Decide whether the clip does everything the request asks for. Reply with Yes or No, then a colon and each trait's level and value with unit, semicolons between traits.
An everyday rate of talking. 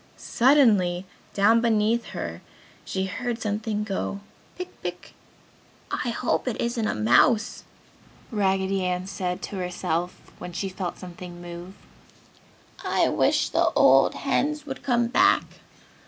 No: slow, 125 wpm